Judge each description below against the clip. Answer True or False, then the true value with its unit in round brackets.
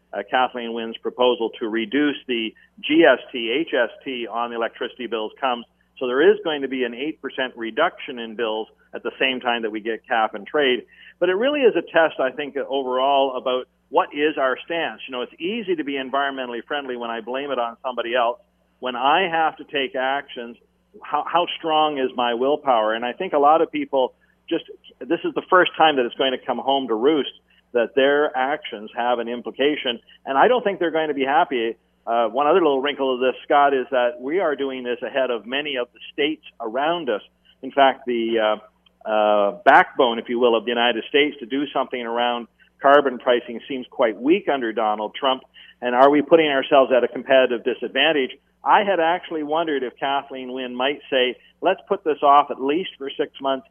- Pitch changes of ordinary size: True (3.6 semitones)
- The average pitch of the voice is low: True (130 Hz)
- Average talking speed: False (210 wpm)